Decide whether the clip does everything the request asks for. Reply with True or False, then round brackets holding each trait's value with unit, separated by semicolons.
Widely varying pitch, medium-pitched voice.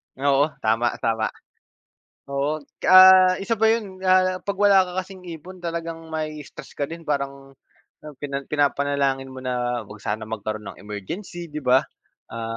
True (6.4 semitones; 145 Hz)